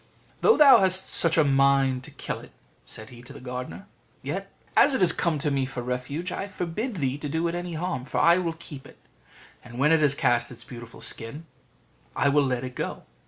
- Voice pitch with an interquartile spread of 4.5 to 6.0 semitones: Yes, average, 5.0 semitones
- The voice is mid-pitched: Yes, medium, 145 Hz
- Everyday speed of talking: No, fast, 215 wpm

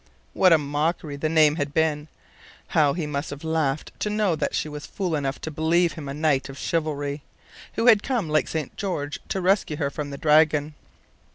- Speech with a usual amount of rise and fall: No, narrow, 2.2 semitones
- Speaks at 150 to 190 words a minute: No, average, 200 wpm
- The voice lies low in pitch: No, medium, 155 Hz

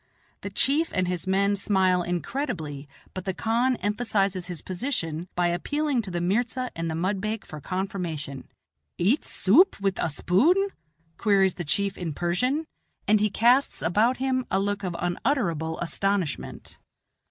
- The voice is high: Yes, high, 195 Hz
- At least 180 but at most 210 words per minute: No, average, 150 wpm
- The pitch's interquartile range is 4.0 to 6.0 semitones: Yes, average, 5.2 semitones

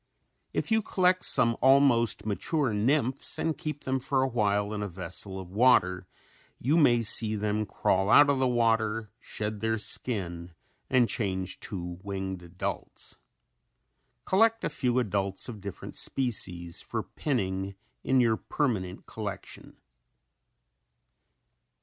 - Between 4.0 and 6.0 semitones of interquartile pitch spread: Yes, average, 5.2 semitones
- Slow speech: Yes, slow, 130 wpm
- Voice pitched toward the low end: Yes, low, 110 Hz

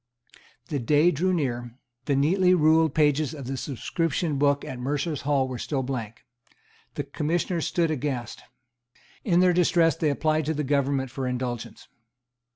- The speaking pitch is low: No, medium, 145 Hz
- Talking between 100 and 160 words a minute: Yes, average, 155 wpm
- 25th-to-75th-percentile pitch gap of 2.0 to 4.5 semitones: Yes, average, 3.4 semitones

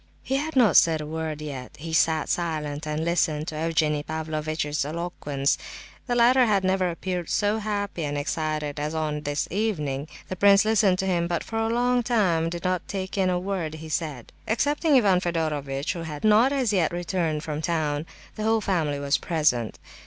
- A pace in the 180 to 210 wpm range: Yes, average, 190 wpm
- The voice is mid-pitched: Yes, medium, 165 Hz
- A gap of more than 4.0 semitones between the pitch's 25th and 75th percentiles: Yes, average, 4.7 semitones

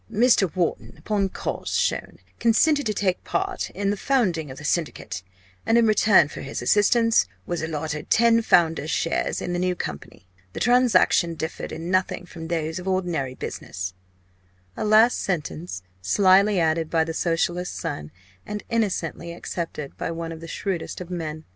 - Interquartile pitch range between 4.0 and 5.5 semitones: Yes, average, 4.4 semitones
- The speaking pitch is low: No, medium, 175 Hz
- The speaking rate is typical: Yes, average, 165 wpm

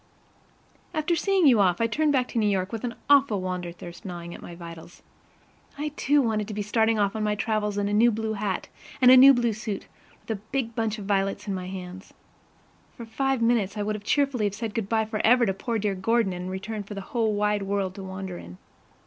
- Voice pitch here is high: Yes, high, 210 Hz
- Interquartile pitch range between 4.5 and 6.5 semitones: No, average, 3.3 semitones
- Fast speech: Yes, fast, 225 wpm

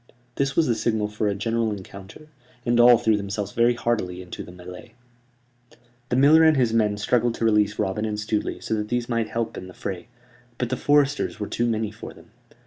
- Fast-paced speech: Yes, fast, 210 wpm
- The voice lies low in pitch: Yes, low, 110 Hz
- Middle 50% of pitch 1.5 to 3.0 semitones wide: Yes, narrow, 2.6 semitones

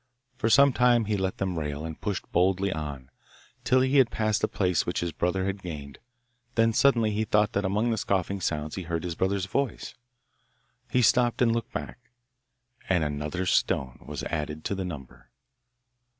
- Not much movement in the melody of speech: No, wide, 5.5 semitones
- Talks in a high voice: No, very low, 95 Hz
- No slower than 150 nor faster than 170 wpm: No, average, 180 wpm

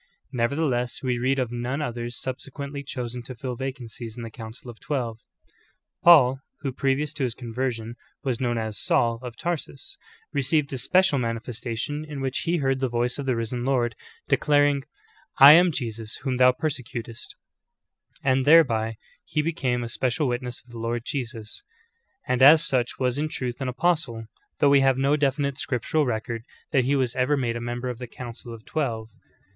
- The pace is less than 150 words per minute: No, average, 180 wpm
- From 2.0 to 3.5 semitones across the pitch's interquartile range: Yes, average, 2.9 semitones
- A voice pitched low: Yes, low, 125 Hz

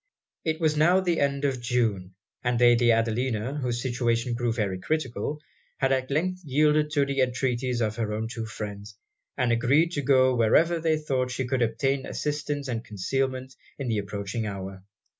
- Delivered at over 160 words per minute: Yes, average, 170 wpm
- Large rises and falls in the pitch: No, average, 3.8 semitones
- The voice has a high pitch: No, low, 125 Hz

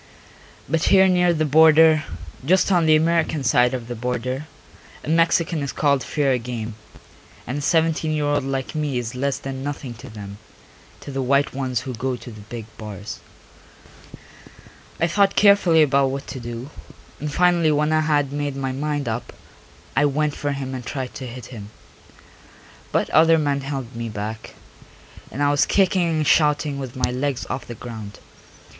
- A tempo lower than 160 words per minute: No, average, 175 wpm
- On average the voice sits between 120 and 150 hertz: Yes, medium, 140 Hz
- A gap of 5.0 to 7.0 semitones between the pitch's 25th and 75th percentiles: No, average, 3.9 semitones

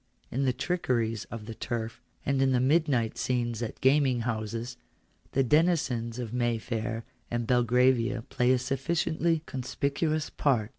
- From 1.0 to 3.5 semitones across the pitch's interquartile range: Yes, average, 2.9 semitones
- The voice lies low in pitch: Yes, low, 125 Hz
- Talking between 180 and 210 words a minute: No, average, 140 wpm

